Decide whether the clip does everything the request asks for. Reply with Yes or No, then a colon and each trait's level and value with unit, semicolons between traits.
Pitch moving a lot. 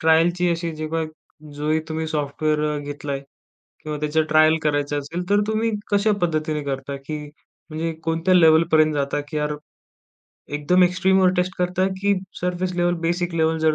No: average, 2.8 semitones